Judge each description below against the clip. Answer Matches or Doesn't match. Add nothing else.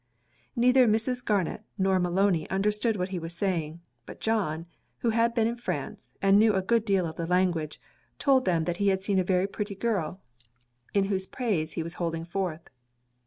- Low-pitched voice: Doesn't match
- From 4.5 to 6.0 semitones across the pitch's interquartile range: Doesn't match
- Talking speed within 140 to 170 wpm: Doesn't match